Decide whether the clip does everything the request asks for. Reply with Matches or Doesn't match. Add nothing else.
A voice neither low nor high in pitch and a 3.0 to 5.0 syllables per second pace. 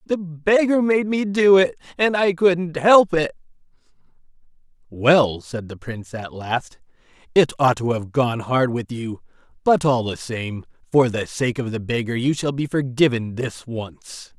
Matches